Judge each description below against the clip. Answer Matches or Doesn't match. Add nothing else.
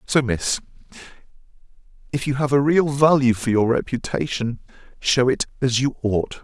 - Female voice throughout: Doesn't match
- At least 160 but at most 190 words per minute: Doesn't match